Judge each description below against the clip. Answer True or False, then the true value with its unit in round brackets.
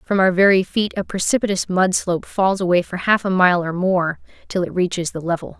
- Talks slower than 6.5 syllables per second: True (5.5 syllables/s)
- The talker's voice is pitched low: False (185 Hz)